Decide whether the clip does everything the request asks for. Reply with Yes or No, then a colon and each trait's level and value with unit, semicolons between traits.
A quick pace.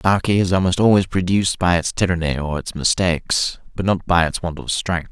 Yes: fast, 210 wpm